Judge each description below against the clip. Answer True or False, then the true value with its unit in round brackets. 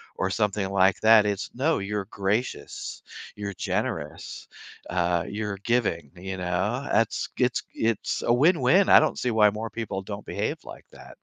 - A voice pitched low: True (105 Hz)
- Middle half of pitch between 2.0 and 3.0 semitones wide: False (3.4 semitones)